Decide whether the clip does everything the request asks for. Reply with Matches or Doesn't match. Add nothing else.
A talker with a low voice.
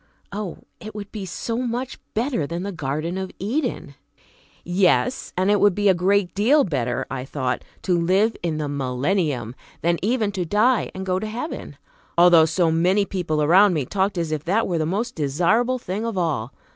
Doesn't match